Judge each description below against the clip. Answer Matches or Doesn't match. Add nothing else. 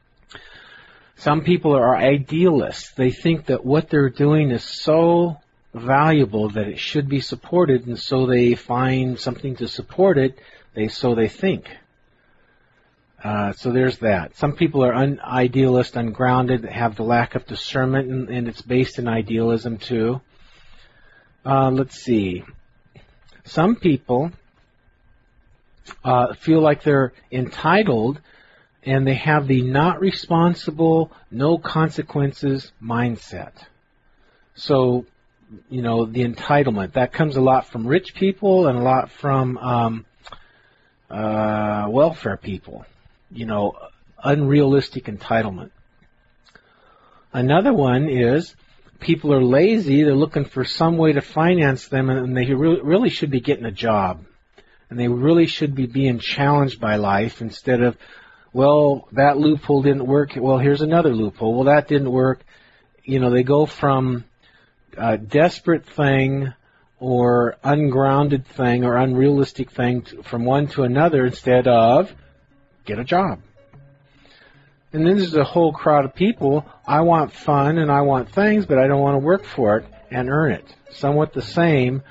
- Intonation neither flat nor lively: Matches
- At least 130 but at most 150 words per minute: Matches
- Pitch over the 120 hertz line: Matches